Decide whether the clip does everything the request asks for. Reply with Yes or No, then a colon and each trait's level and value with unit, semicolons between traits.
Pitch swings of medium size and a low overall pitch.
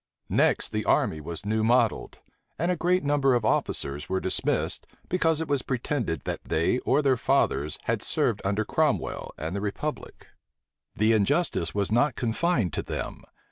No: wide, 7.2 semitones; low, 115 Hz